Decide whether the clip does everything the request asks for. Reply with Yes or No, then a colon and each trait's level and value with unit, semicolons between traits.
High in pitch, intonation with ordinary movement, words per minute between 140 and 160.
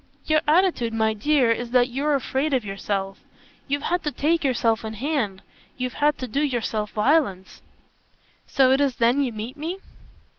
No: very high, 255 Hz; average, 4.9 semitones; average, 175 wpm